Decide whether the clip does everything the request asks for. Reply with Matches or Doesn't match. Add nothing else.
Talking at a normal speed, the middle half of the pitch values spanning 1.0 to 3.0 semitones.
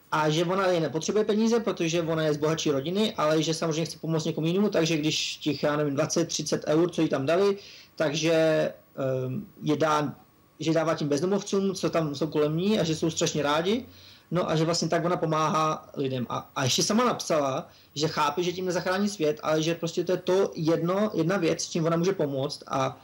Doesn't match